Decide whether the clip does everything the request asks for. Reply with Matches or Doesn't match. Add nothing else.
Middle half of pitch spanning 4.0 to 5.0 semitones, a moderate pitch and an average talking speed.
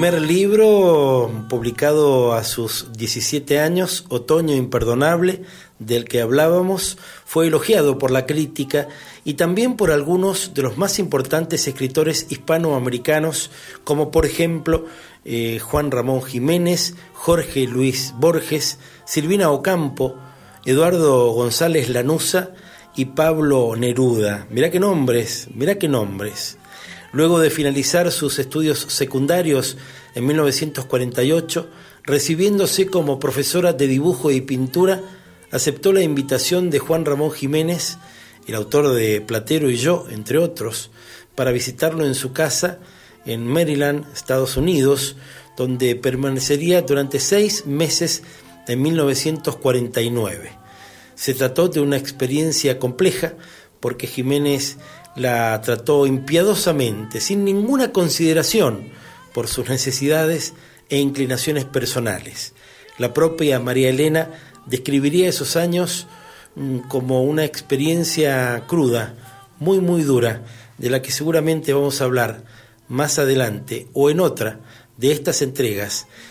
Doesn't match